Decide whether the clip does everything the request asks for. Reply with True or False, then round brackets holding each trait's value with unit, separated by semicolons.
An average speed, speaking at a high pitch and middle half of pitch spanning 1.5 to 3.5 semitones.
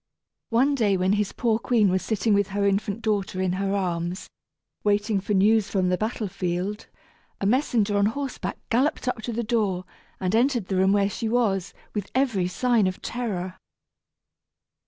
True (175 wpm; 205 Hz; 3.2 semitones)